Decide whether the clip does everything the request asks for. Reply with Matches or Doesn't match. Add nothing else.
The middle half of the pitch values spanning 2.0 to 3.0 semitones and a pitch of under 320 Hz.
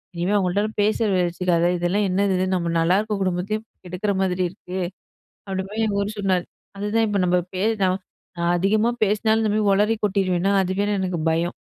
Matches